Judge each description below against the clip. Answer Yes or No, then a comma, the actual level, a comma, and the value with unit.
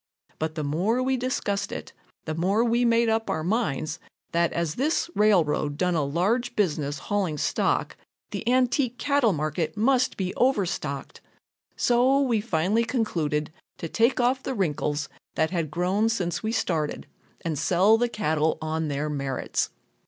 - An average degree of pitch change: No, wide, 7.0 semitones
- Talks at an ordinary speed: Yes, average, 155 wpm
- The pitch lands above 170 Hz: Yes, high, 190 Hz